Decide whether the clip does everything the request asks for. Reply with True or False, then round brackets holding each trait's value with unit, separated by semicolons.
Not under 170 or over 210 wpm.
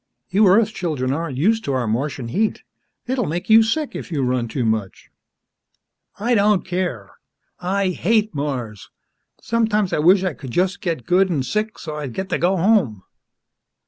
True (175 wpm)